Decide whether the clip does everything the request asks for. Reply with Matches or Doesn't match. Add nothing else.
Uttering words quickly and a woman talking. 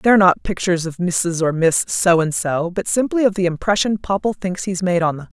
Matches